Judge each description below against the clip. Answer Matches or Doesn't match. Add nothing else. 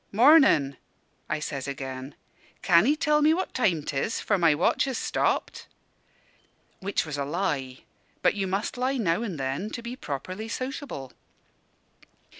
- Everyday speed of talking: Matches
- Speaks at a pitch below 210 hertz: Matches